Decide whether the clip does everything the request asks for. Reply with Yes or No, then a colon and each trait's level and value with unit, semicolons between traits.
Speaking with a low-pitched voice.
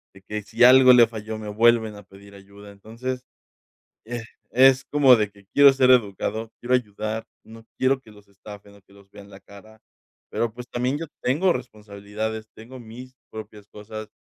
Yes: low, 110 Hz